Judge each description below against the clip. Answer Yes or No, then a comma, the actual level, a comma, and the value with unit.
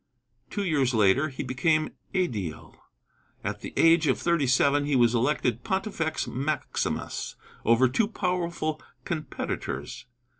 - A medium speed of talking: No, slow, 120 wpm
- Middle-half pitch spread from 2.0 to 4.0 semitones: No, average, 5.0 semitones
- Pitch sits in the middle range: Yes, medium, 150 Hz